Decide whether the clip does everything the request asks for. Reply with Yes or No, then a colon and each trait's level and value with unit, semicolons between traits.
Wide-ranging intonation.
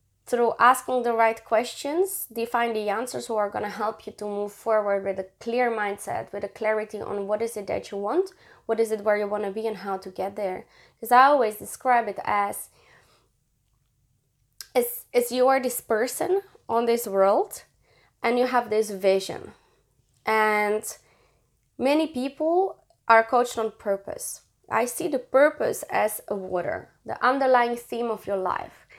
No: average, 3.3 semitones